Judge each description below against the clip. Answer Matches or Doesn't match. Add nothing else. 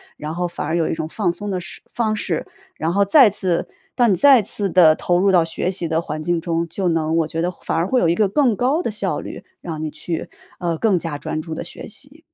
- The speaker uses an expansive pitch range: Doesn't match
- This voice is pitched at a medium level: Matches